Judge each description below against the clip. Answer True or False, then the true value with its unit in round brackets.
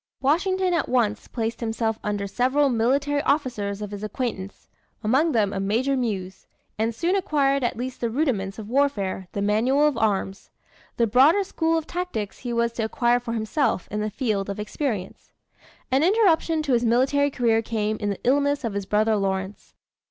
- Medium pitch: False (235 Hz)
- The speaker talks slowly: False (180 wpm)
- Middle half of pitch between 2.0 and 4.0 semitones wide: False (5.2 semitones)